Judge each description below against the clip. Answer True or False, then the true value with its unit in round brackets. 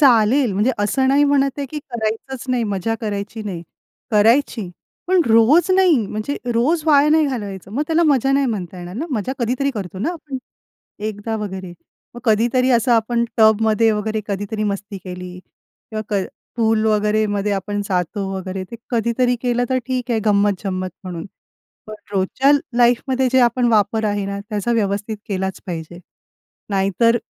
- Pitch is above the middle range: True (220 Hz)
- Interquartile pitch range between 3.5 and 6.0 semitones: True (4.0 semitones)